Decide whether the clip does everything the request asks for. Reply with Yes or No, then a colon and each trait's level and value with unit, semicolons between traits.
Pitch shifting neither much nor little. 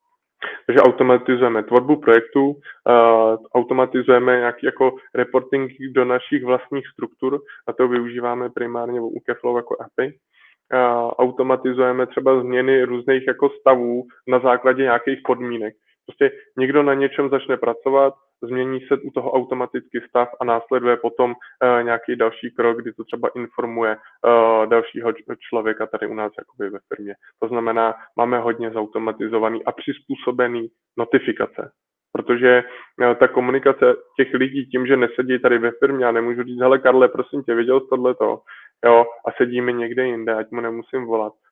No: narrow, 1.8 semitones